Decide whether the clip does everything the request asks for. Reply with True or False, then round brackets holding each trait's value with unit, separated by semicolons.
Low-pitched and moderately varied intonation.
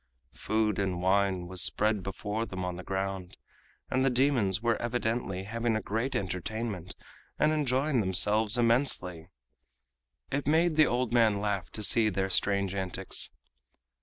True (105 Hz; 4.0 semitones)